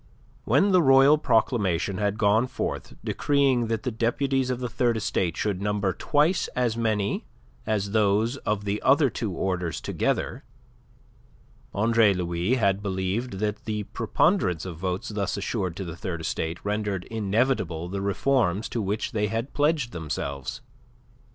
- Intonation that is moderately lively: Yes, average, 4.1 semitones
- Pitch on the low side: Yes, low, 105 Hz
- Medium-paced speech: Yes, average, 150 wpm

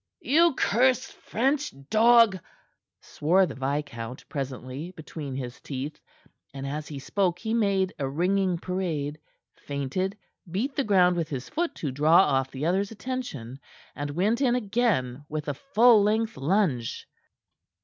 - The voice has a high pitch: No, medium, 180 Hz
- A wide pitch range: Yes, wide, 7.7 semitones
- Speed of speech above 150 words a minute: No, average, 140 wpm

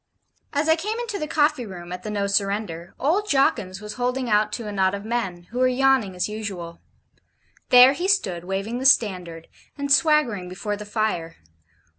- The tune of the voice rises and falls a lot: Yes, wide, 6.1 semitones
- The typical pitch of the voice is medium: No, high, 215 Hz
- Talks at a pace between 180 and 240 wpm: Yes, average, 185 wpm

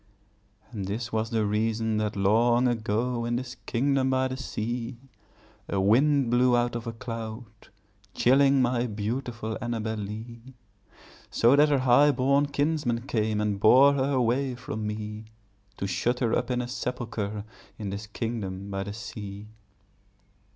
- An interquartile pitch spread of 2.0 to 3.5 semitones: Yes, average, 3.0 semitones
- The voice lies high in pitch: No, low, 115 Hz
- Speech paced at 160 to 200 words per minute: No, average, 150 wpm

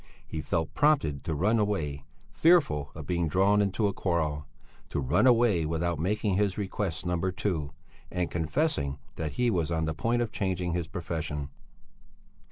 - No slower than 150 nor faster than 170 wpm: Yes, average, 165 wpm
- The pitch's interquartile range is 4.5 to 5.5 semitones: Yes, average, 4.8 semitones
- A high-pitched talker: No, very low, 85 Hz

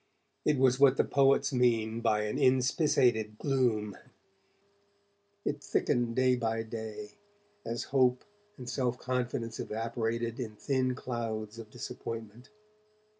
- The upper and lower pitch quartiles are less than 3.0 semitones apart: Yes, narrow, 2.5 semitones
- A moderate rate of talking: No, slow, 120 wpm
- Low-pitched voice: Yes, low, 120 Hz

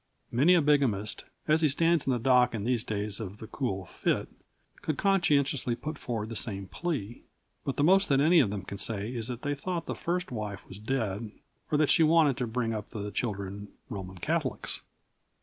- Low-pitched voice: Yes, low, 120 Hz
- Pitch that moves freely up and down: Yes, wide, 6.1 semitones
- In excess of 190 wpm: Yes, average, 200 wpm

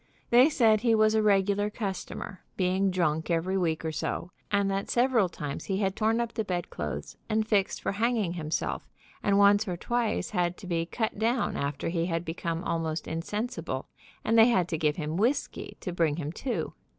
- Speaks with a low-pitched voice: No, high, 190 Hz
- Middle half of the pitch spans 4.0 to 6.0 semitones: Yes, average, 4.6 semitones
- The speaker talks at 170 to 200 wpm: Yes, average, 190 wpm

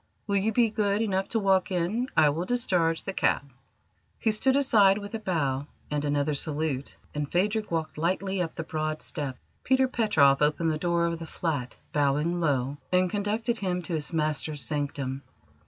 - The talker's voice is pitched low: No, medium, 170 Hz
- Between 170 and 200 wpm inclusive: Yes, average, 180 wpm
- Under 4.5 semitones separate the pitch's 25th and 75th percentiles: No, average, 5.3 semitones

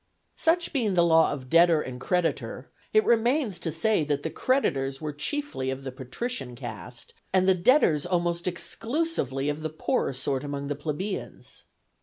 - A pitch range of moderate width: No, wide, 7.7 semitones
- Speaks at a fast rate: No, average, 165 wpm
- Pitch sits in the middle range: Yes, medium, 165 Hz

